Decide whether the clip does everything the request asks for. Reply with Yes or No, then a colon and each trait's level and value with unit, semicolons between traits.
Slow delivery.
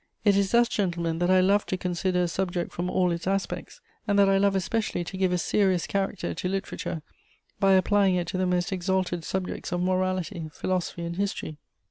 No: average, 200 wpm